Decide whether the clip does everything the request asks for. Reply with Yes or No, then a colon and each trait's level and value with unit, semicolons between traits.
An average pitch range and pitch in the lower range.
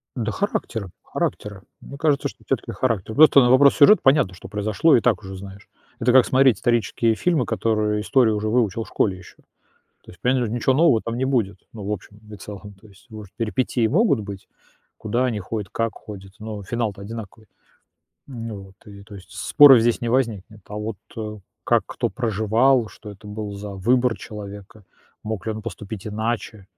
Yes: average, 3.0 semitones; low, 110 Hz